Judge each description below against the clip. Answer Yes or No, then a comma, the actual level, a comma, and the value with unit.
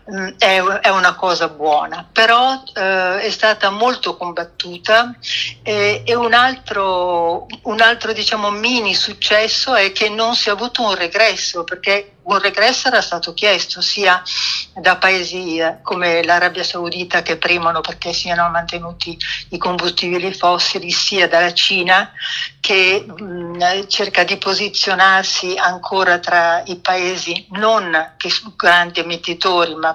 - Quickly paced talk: No, average, 130 wpm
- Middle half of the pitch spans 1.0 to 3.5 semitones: Yes, average, 3.0 semitones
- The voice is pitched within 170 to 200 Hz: Yes, medium, 185 Hz